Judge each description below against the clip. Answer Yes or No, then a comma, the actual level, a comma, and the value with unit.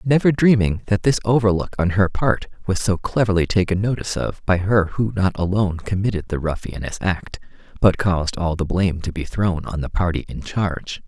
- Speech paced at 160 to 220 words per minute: Yes, average, 195 wpm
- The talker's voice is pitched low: Yes, very low, 95 Hz